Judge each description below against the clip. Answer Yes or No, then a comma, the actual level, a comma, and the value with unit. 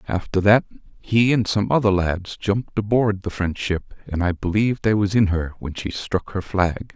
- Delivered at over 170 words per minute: Yes, fast, 205 wpm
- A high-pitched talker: No, low, 100 Hz